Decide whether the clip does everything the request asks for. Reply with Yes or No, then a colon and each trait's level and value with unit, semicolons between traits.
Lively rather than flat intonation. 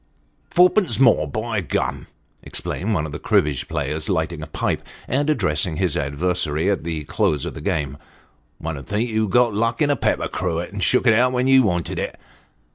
Yes: wide, 7.6 semitones